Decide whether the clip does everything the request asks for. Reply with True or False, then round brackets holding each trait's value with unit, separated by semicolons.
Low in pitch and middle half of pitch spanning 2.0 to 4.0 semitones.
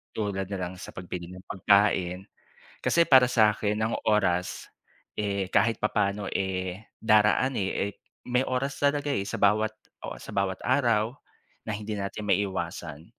True (105 Hz; 2.6 semitones)